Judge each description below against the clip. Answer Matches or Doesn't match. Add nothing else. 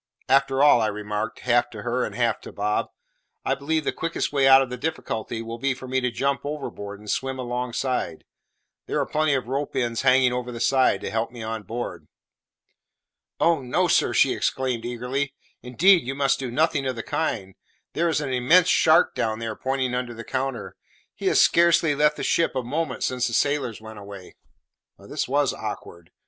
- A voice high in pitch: Doesn't match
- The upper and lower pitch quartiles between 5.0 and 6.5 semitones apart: Doesn't match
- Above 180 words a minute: Matches